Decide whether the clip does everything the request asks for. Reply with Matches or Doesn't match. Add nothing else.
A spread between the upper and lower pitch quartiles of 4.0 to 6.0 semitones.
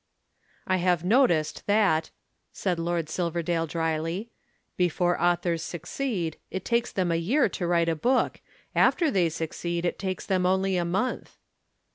Doesn't match